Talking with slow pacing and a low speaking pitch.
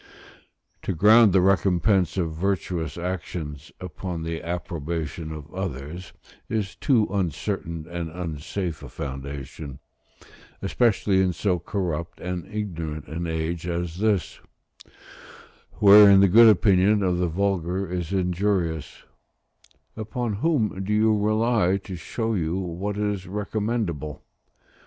Yes: slow, 120 wpm; very low, 90 Hz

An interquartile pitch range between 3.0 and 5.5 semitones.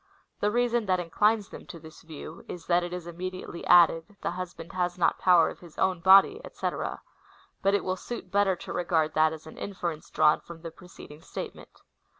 No: narrow, 2.6 semitones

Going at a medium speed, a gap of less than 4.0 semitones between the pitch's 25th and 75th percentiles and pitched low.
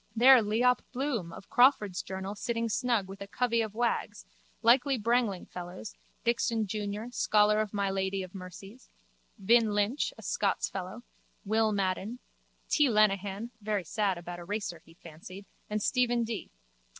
No: average, 150 wpm; average, 3.4 semitones; high, 210 Hz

